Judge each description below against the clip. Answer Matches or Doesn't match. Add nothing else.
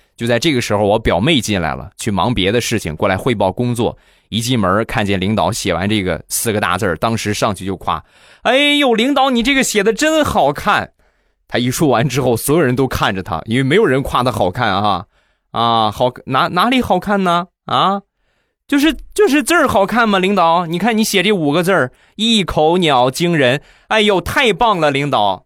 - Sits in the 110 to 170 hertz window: Matches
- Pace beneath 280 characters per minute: Doesn't match